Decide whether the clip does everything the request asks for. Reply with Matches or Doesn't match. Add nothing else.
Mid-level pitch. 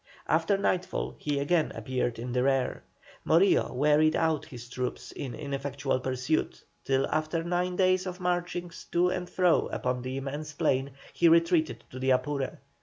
Matches